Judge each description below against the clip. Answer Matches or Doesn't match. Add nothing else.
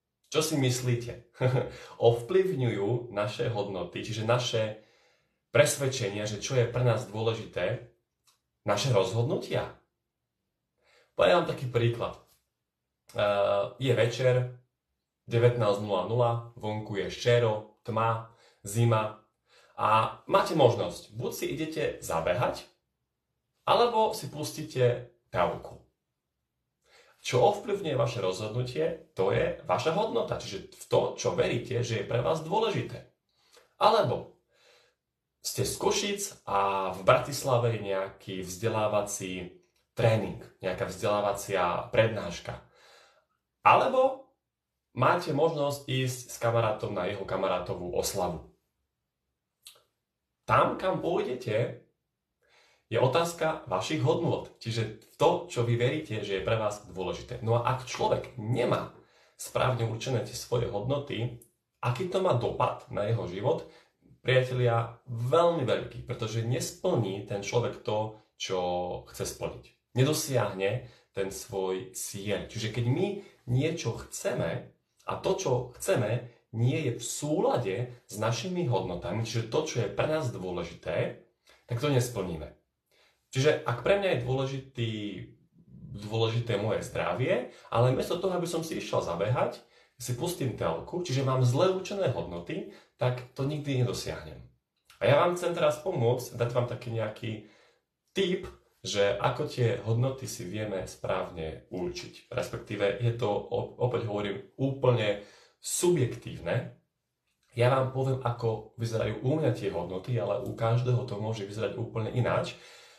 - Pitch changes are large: Doesn't match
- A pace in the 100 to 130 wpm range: Matches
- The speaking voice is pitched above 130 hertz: Doesn't match